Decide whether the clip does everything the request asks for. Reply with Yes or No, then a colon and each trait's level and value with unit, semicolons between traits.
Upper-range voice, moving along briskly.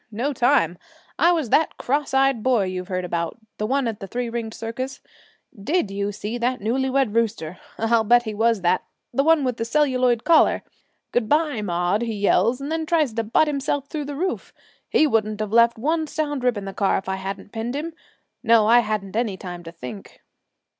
Yes: high, 230 Hz; fast, 210 wpm